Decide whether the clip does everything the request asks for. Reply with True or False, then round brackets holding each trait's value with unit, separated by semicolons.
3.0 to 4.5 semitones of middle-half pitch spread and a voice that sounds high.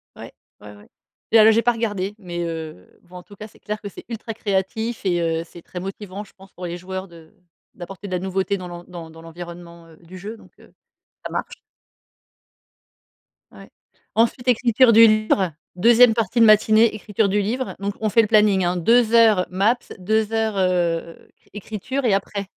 True (3.7 semitones; 200 Hz)